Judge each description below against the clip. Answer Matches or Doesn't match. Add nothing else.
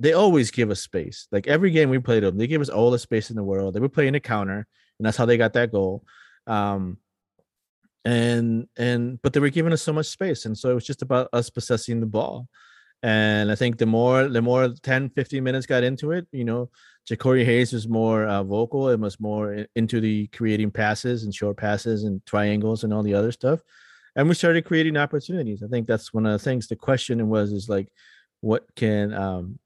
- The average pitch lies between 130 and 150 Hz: Doesn't match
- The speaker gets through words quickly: Matches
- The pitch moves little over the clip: Doesn't match